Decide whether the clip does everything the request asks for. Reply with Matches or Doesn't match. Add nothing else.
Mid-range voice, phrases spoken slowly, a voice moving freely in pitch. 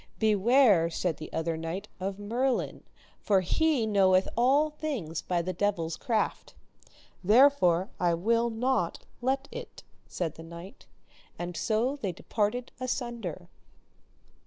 Doesn't match